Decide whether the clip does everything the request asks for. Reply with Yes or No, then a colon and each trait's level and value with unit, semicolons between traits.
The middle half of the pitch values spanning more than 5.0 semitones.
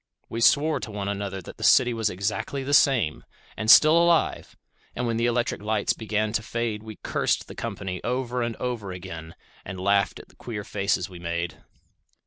No: average, 3.7 semitones